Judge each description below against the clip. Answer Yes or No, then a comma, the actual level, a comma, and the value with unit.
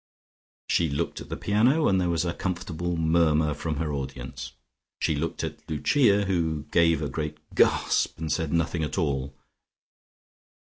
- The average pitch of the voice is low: Yes, very low, 80 Hz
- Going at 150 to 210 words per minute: Yes, average, 155 wpm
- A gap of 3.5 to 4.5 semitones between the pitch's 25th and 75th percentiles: No, narrow, 2.6 semitones